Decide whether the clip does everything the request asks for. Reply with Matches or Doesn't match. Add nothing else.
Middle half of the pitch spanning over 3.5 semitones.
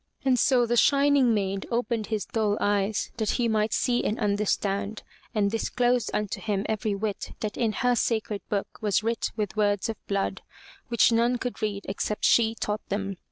Doesn't match